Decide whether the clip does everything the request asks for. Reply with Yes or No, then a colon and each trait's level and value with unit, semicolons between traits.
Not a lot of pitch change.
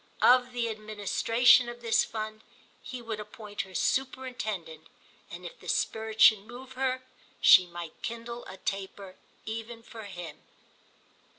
No: average, 3.0 semitones